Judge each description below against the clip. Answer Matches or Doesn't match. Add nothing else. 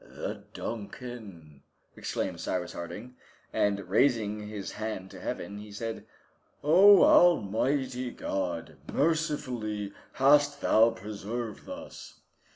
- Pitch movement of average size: Matches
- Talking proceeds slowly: Matches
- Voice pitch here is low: Matches